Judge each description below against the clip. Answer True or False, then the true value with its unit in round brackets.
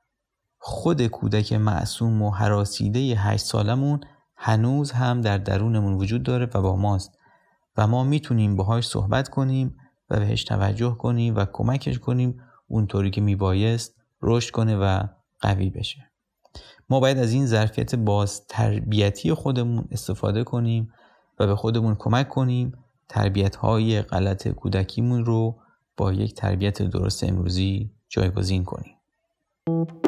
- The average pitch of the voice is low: True (110 Hz)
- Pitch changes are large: False (3.4 semitones)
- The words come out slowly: False (130 wpm)